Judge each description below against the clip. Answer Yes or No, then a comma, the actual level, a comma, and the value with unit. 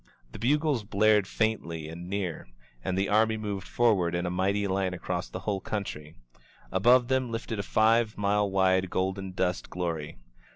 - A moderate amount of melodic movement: Yes, average, 3.0 semitones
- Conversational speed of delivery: Yes, average, 170 wpm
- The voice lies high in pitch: No, low, 100 Hz